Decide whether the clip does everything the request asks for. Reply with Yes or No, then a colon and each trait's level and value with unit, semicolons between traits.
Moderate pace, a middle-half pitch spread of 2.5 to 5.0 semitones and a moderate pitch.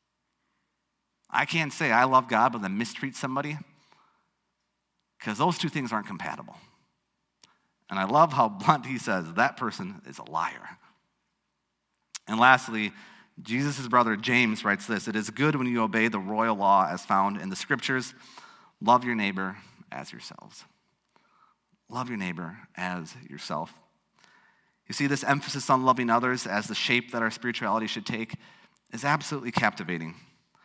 No: average, 150 wpm; average, 4.4 semitones; low, 125 Hz